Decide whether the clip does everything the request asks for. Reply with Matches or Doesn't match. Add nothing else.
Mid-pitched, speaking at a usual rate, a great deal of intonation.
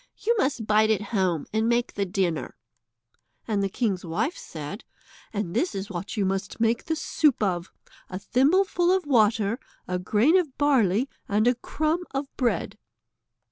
Doesn't match